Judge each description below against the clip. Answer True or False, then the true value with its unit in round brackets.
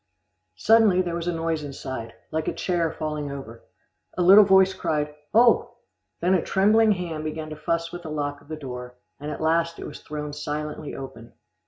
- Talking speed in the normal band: True (190 wpm)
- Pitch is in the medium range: True (155 Hz)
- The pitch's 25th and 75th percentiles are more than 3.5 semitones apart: False (3.1 semitones)